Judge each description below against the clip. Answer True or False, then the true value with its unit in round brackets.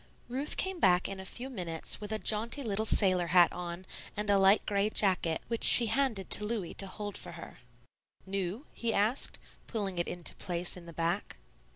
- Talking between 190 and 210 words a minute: True (195 wpm)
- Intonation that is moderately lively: True (3.8 semitones)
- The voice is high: True (200 Hz)